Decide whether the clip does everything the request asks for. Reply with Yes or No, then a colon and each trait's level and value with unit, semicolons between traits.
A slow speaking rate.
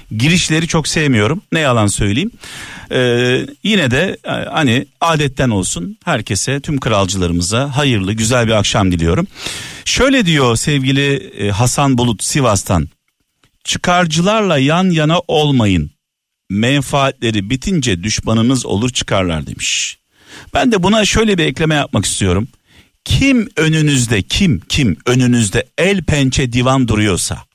No: average, 115 wpm